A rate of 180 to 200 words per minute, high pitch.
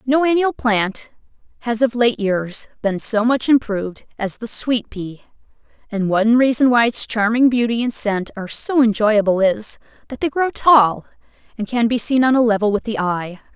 Yes: average, 185 wpm; high, 230 Hz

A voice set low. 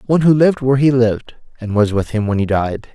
Yes: low, 120 Hz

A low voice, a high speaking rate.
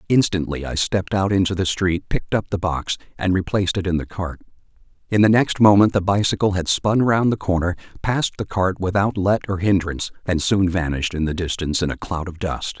Yes: very low, 95 Hz; fast, 215 wpm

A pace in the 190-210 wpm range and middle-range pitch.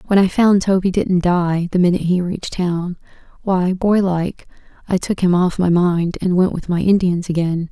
Yes: average, 195 wpm; medium, 180 Hz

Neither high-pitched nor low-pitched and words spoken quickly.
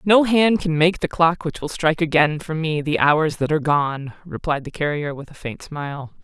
Yes: medium, 155 Hz; fast, 230 wpm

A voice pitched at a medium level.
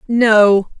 No: high, 215 Hz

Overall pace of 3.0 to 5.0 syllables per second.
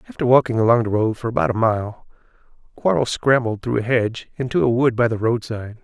No: 6.2 syllables/s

